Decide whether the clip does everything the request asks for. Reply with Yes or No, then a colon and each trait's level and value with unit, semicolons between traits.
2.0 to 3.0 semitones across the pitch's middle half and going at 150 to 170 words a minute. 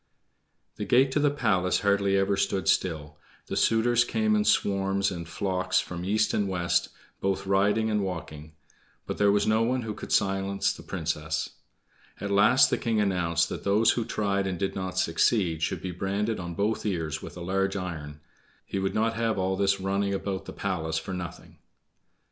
No: narrow, 2.6 semitones; average, 185 wpm